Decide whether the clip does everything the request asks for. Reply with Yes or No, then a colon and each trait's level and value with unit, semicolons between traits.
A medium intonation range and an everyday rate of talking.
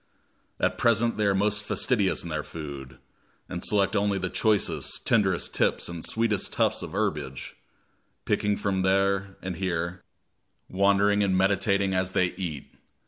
No: narrow, 2.1 semitones; average, 145 wpm